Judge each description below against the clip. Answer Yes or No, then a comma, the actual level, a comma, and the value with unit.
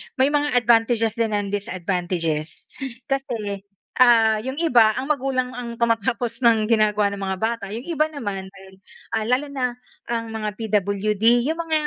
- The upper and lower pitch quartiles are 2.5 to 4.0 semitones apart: Yes, average, 3.4 semitones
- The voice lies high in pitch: Yes, high, 225 Hz